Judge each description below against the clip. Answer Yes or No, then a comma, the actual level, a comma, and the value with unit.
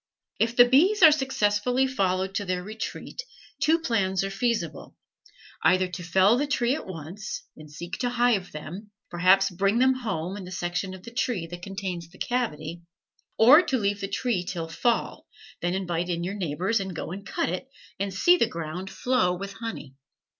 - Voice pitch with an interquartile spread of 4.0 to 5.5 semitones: Yes, average, 5.0 semitones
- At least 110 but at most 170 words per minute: No, average, 180 wpm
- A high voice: Yes, high, 195 Hz